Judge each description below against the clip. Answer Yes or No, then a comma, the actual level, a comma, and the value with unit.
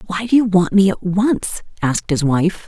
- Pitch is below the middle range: No, high, 190 Hz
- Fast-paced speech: Yes, fast, 225 wpm